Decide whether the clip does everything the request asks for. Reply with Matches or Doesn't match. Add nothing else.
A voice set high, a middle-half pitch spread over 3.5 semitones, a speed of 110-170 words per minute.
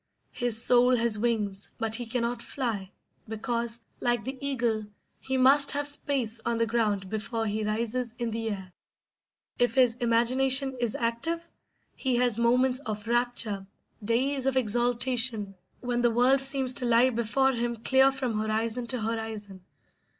Doesn't match